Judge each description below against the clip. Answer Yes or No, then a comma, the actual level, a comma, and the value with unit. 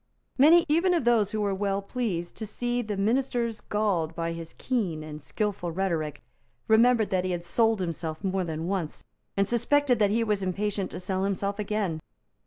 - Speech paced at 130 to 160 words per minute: No, average, 185 wpm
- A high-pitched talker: Yes, high, 200 Hz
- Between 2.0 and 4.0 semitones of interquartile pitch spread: No, average, 4.4 semitones